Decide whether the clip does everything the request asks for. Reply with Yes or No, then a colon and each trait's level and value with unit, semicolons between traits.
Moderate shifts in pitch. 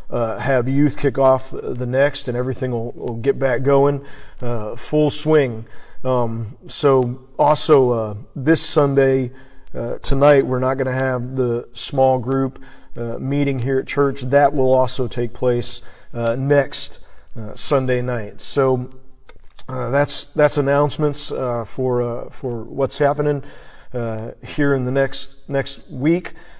No: narrow, 2.3 semitones